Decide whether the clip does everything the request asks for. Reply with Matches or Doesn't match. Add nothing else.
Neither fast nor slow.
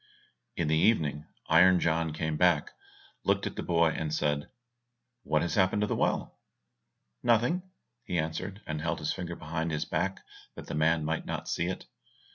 Matches